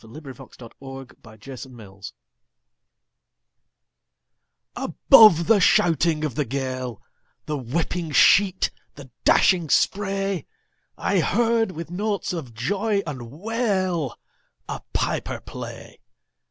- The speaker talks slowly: Yes, slow, 95 wpm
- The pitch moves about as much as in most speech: No, wide, 7.2 semitones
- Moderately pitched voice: Yes, medium, 155 Hz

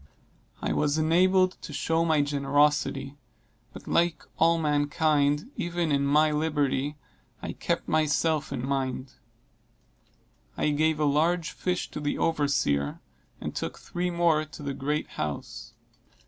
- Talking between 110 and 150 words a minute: Yes, slow, 135 wpm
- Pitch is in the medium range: Yes, medium, 150 Hz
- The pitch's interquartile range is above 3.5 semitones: No, narrow, 2.5 semitones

